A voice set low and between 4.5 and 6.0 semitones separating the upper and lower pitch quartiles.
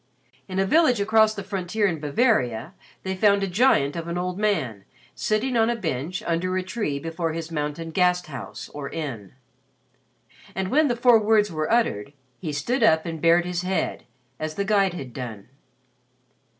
No: medium, 180 Hz; average, 5.2 semitones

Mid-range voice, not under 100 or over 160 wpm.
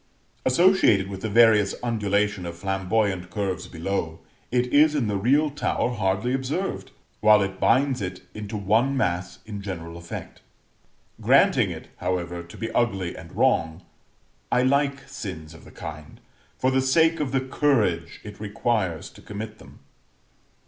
No: low, 105 Hz; average, 150 wpm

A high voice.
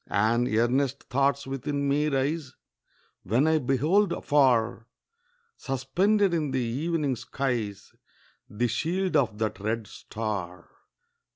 No: low, 135 Hz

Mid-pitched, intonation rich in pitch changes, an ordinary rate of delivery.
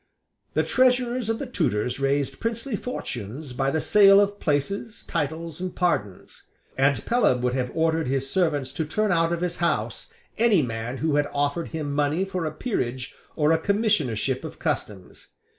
Yes: medium, 160 Hz; wide, 6.6 semitones; average, 170 wpm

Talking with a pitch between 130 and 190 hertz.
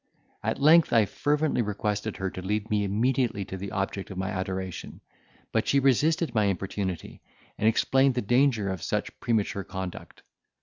No: low, 105 Hz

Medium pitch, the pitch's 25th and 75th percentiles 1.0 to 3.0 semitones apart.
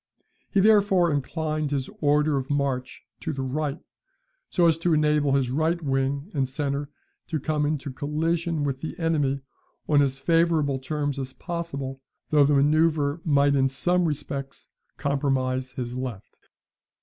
Yes: medium, 145 Hz; narrow, 2.6 semitones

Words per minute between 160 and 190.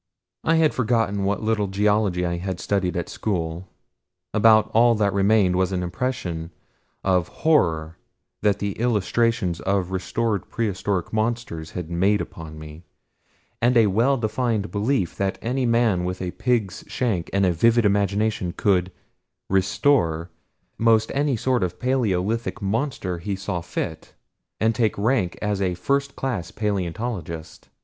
No: average, 140 wpm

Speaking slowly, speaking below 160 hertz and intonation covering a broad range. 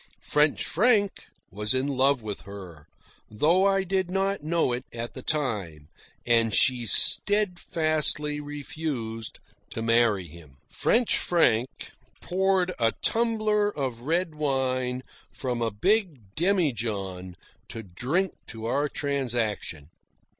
Yes: slow, 120 wpm; low, 135 Hz; wide, 7.7 semitones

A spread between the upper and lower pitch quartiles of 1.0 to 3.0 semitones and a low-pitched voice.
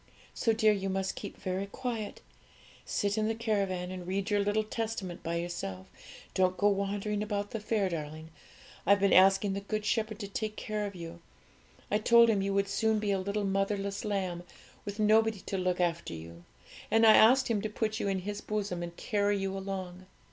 No: narrow, 2.4 semitones; high, 200 Hz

